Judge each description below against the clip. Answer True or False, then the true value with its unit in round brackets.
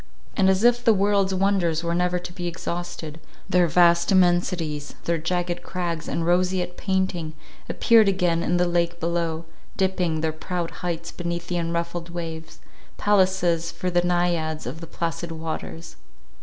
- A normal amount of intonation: False (1.6 semitones)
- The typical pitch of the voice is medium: True (175 Hz)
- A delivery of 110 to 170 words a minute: True (150 wpm)